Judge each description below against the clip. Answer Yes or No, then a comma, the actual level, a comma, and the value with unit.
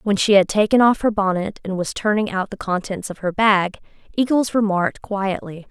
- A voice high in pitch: Yes, high, 200 Hz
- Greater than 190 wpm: Yes, average, 200 wpm